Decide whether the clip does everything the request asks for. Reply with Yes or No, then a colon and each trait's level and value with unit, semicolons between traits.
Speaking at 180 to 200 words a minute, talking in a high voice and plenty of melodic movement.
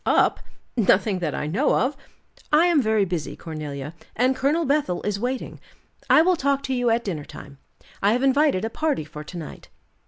Yes: average, 190 wpm; high, 225 Hz; wide, 8.3 semitones